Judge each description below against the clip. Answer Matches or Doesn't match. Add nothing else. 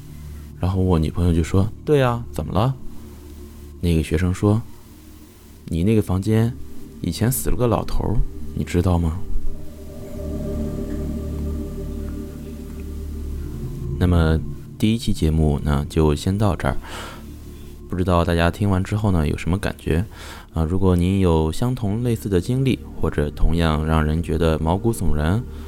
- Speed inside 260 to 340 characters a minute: Doesn't match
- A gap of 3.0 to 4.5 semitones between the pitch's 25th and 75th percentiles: Matches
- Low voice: Matches